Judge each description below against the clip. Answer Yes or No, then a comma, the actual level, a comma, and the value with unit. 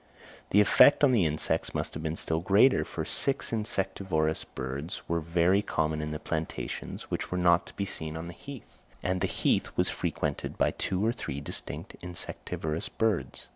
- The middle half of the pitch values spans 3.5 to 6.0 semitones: Yes, average, 4.1 semitones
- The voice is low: Yes, very low, 85 Hz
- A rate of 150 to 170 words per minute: No, average, 180 wpm